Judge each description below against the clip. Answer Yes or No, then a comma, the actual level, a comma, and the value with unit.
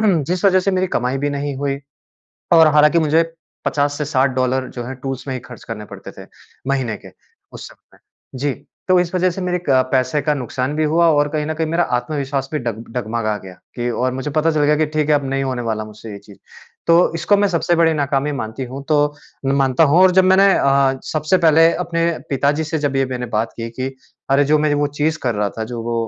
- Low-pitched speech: No, medium, 145 Hz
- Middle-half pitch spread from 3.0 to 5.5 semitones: Yes, average, 3.8 semitones